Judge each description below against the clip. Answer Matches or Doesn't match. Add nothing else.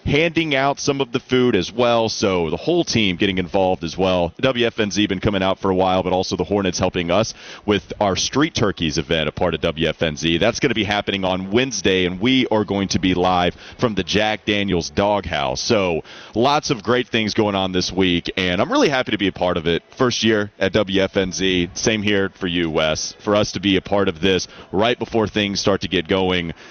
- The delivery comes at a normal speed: Doesn't match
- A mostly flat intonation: Doesn't match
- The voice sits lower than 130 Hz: Matches